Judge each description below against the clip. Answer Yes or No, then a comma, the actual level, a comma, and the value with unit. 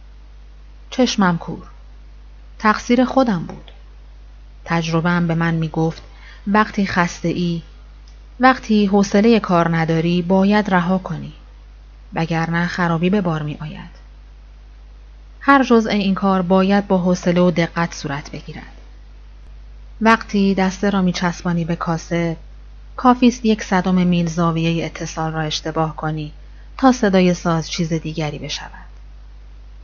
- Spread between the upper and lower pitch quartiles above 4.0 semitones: No, average, 3.7 semitones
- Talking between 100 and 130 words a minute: Yes, average, 120 wpm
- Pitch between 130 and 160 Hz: No, medium, 170 Hz